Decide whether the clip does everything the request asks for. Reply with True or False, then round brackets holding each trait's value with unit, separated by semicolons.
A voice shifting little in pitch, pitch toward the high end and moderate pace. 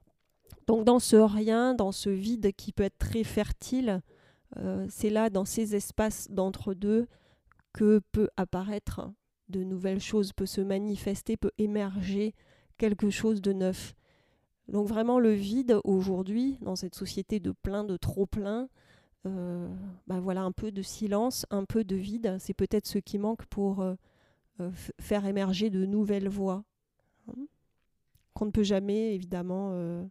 True (2.2 semitones; 200 Hz; 155 wpm)